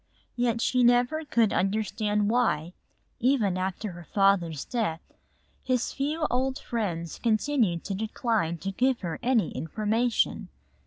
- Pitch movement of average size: Yes, average, 4.5 semitones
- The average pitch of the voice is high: Yes, high, 220 Hz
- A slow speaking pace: Yes, slow, 125 wpm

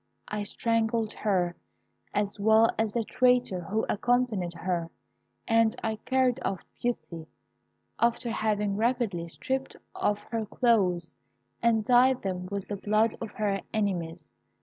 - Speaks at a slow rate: Yes, slow, 130 wpm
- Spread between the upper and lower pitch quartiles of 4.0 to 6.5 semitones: No, average, 3.3 semitones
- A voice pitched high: Yes, high, 215 Hz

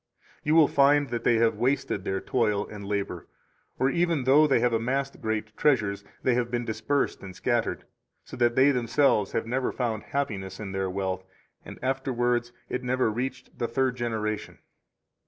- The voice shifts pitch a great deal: No, average, 3.6 semitones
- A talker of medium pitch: No, low, 120 Hz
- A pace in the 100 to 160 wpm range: No, average, 175 wpm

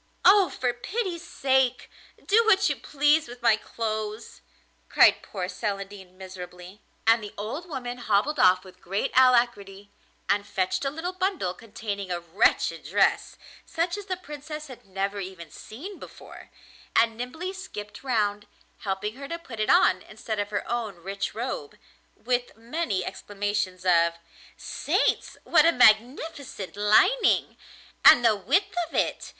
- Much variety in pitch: Yes, wide, 6.4 semitones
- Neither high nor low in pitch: No, high, 225 Hz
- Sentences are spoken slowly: No, average, 145 wpm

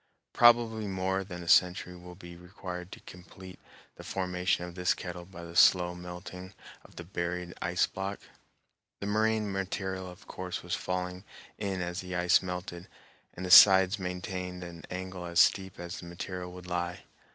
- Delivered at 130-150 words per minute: No, average, 170 wpm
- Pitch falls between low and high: No, very low, 90 Hz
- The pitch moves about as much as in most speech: No, narrow, 1.2 semitones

